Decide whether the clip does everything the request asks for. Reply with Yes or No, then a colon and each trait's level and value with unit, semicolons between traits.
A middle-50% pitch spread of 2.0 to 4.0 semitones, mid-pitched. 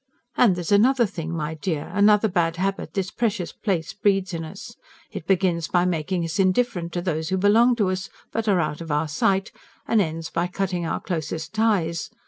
Yes: average, 3.5 semitones; medium, 180 Hz